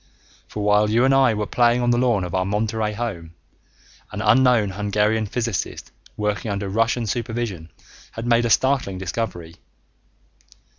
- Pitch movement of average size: Yes, average, 3.0 semitones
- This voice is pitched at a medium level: No, low, 110 Hz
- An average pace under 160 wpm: Yes, average, 150 wpm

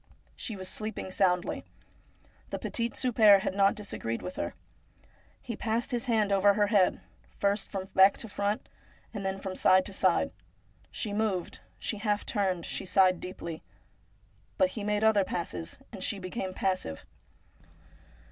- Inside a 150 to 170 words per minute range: Yes, average, 155 wpm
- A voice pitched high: Yes, high, 200 Hz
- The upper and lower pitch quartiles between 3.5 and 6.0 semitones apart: No, narrow, 2.4 semitones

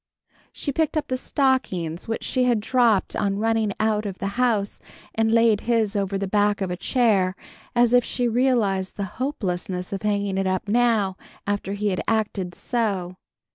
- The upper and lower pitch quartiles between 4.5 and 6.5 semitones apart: No, average, 3.6 semitones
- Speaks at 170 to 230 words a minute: Yes, average, 175 wpm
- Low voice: No, high, 210 Hz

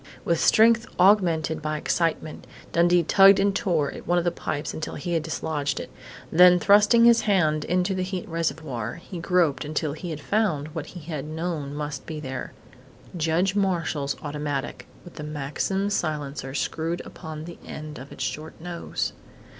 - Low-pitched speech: No, medium, 160 Hz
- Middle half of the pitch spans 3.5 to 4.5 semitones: No, average, 3.1 semitones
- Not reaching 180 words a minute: Yes, average, 170 wpm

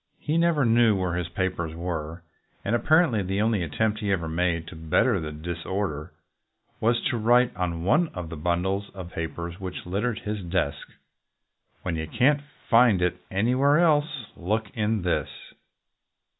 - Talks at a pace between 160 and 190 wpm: Yes, average, 165 wpm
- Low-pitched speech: Yes, very low, 95 Hz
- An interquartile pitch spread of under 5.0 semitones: No, average, 5.3 semitones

